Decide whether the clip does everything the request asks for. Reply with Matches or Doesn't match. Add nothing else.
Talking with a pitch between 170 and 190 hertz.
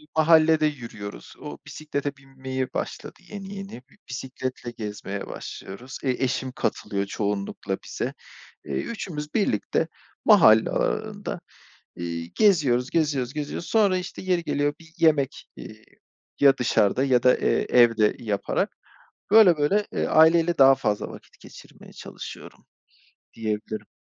Doesn't match